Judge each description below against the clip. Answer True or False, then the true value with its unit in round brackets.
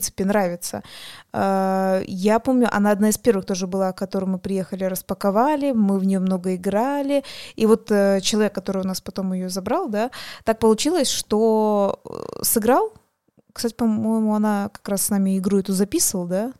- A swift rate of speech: True (165 wpm)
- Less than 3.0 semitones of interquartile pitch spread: True (2.6 semitones)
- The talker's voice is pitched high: True (205 Hz)